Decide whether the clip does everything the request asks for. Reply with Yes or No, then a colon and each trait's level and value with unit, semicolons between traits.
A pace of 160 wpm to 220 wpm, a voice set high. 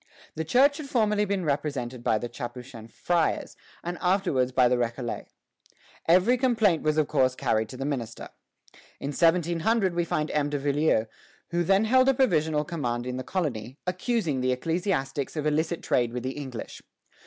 No: average, 175 wpm; medium, 150 Hz